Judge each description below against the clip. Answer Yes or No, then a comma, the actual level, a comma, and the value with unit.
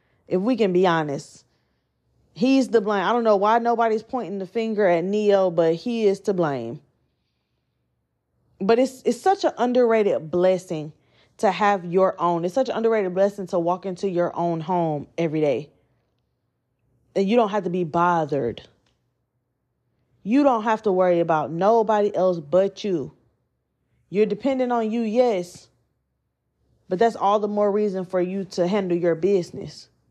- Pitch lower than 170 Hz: No, medium, 185 Hz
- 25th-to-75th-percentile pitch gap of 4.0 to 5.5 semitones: Yes, average, 5.0 semitones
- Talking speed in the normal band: Yes, average, 160 wpm